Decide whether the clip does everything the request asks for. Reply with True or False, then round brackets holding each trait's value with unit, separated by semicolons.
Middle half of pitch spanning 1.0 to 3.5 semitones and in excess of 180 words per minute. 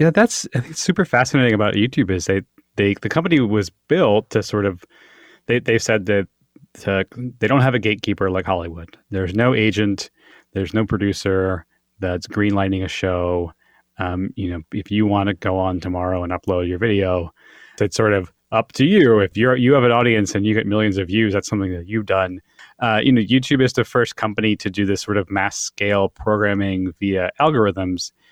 True (2.9 semitones; 200 wpm)